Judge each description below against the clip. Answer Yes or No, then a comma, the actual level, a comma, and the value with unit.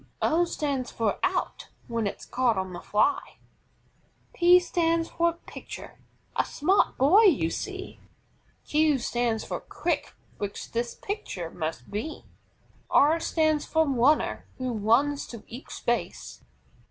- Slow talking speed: Yes, slow, 130 wpm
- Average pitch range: No, wide, 6.4 semitones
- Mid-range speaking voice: No, very high, 280 Hz